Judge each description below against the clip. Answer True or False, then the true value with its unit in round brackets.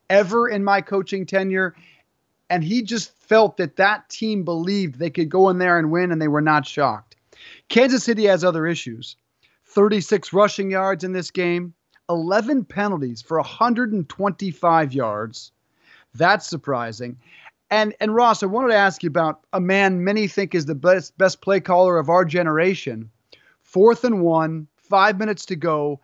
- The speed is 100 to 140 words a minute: False (165 wpm)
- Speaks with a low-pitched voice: False (185 Hz)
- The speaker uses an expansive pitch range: False (4.1 semitones)